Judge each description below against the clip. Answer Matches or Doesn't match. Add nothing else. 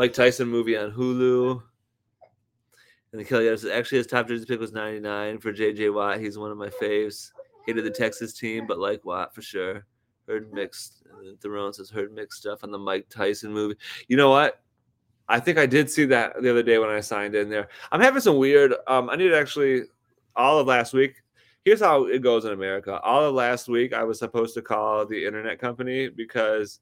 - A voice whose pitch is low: Matches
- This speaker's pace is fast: Matches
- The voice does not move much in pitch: Doesn't match